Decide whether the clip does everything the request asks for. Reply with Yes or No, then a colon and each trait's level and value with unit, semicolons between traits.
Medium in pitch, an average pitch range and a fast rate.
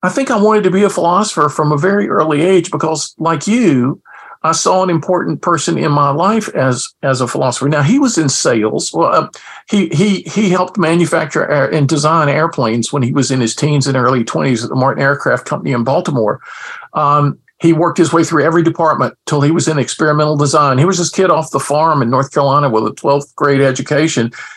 Yes: medium, 150 Hz; average, 3.6 semitones; fast, 215 wpm